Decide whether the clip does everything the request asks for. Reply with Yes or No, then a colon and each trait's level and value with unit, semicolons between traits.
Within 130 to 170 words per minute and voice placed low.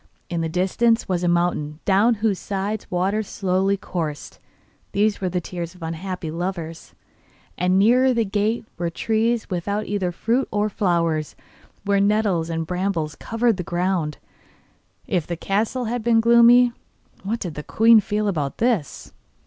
No: average, 155 wpm; high, 195 Hz